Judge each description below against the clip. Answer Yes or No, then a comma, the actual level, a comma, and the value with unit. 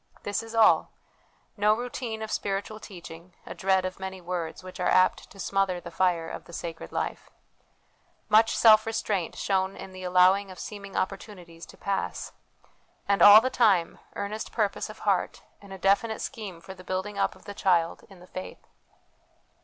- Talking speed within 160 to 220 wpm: Yes, average, 175 wpm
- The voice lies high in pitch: Yes, high, 195 Hz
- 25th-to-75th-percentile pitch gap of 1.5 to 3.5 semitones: Yes, narrow, 2.5 semitones